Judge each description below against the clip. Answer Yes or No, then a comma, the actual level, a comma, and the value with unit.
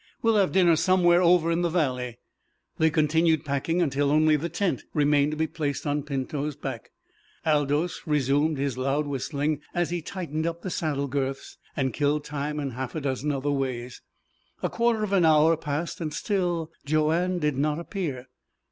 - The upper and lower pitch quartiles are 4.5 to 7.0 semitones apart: No, average, 3.1 semitones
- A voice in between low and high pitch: Yes, medium, 150 Hz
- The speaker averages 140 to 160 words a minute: No, average, 175 wpm